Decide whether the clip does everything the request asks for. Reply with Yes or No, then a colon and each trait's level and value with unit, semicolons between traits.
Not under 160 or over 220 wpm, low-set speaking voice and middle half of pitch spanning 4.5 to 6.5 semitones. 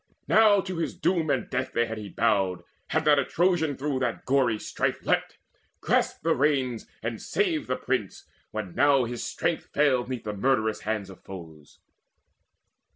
Yes: average, 170 wpm; low, 130 Hz; wide, 5.6 semitones